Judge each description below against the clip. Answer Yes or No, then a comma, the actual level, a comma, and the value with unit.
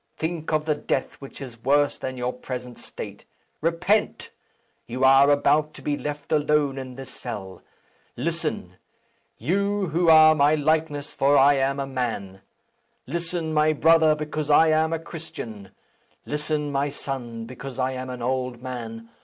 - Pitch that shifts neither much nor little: Yes, average, 3.4 semitones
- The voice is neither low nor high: Yes, medium, 145 Hz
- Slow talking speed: No, average, 155 wpm